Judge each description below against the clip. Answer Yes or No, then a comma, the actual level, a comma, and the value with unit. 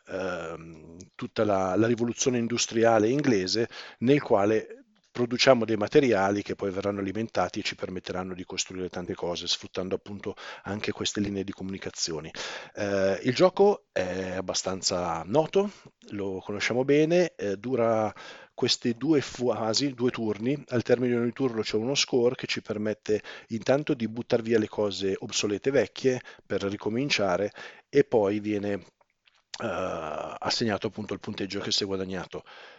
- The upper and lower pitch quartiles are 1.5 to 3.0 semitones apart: No, average, 3.9 semitones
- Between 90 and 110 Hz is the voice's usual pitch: Yes, low, 105 Hz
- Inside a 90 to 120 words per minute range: No, average, 145 wpm